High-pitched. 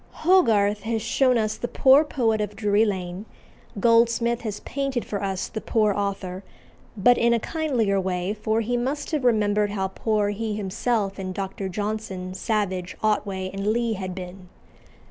Yes: high, 210 Hz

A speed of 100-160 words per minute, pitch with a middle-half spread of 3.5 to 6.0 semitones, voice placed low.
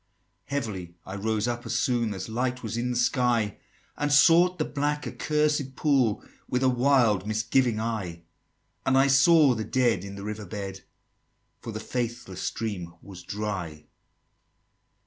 Yes: average, 155 wpm; average, 4.4 semitones; low, 115 Hz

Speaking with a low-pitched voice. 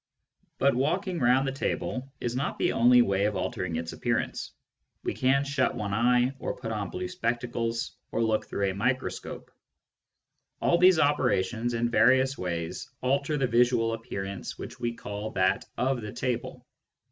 Yes: low, 120 Hz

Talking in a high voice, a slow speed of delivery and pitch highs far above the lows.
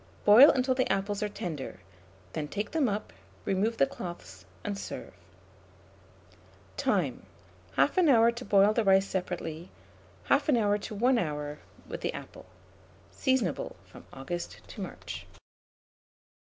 Yes: high, 200 Hz; slow, 130 wpm; wide, 6.0 semitones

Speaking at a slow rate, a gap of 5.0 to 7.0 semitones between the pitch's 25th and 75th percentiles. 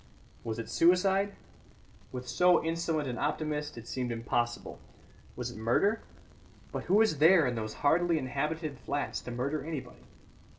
No: average, 145 wpm; average, 5.3 semitones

